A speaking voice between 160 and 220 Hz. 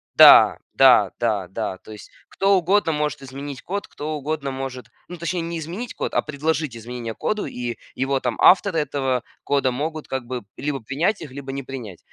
No: medium, 140 Hz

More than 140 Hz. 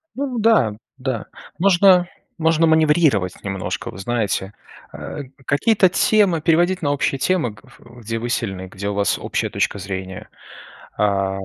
No: low, 130 Hz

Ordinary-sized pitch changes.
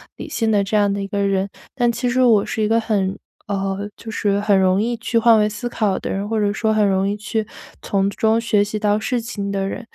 No: narrow, 2.2 semitones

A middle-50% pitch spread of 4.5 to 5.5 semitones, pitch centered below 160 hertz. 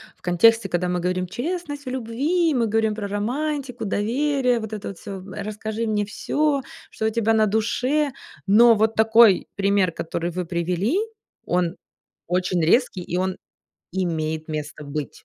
No: average, 4.8 semitones; high, 215 Hz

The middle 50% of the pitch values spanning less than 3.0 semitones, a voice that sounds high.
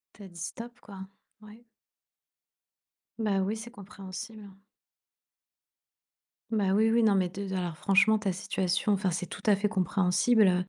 Yes: narrow, 2.6 semitones; high, 200 Hz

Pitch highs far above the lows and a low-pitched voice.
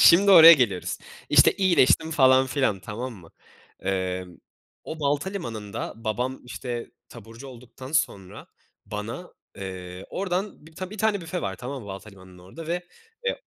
Yes: wide, 8.6 semitones; low, 125 Hz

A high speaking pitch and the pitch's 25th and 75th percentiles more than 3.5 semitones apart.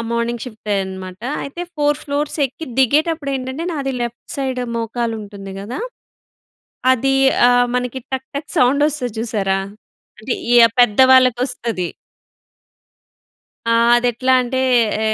No: very high, 250 Hz; average, 2.9 semitones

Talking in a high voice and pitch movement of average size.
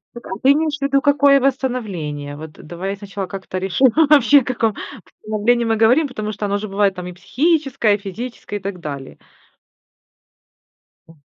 No: high, 215 Hz; wide, 5.8 semitones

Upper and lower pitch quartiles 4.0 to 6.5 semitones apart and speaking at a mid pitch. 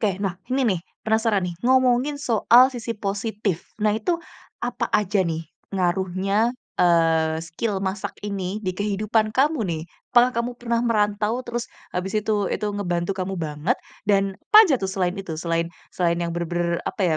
No: average, 4.3 semitones; high, 200 Hz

